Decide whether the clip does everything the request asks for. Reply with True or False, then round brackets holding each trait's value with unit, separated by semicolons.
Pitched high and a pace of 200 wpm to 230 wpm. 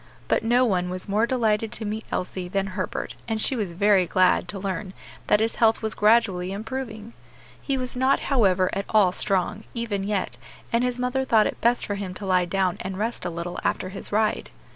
True (210 Hz; 205 wpm)